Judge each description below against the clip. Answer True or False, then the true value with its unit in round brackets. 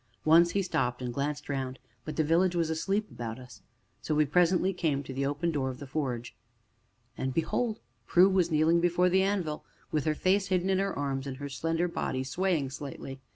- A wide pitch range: False (4.8 semitones)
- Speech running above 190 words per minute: True (205 wpm)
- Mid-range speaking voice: True (155 Hz)